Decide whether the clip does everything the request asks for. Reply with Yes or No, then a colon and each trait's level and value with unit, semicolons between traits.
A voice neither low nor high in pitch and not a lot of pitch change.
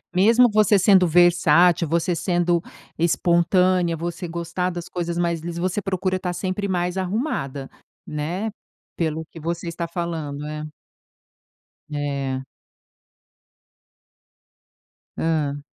Yes: medium, 170 Hz; narrow, 2.2 semitones